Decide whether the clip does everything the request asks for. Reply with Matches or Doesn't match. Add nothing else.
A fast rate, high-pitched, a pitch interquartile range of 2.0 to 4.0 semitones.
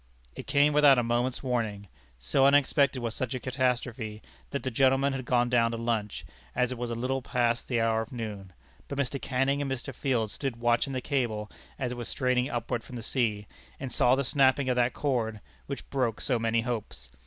Doesn't match